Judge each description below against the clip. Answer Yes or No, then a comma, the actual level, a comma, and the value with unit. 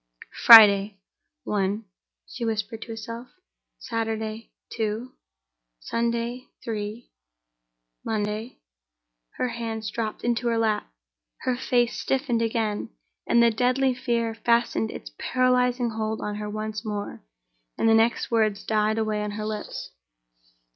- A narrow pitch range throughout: Yes, narrow, 1.8 semitones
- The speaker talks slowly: Yes, slow, 120 wpm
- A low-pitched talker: No, high, 225 Hz